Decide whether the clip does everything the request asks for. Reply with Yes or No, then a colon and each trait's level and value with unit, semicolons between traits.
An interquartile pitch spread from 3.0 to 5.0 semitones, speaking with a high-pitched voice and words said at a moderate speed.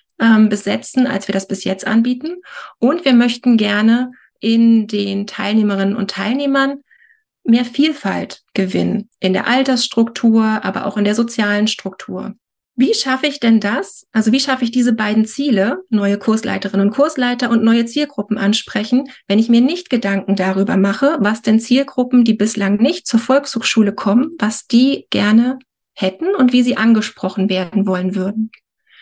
Yes: average, 3.7 semitones; high, 225 Hz; average, 155 wpm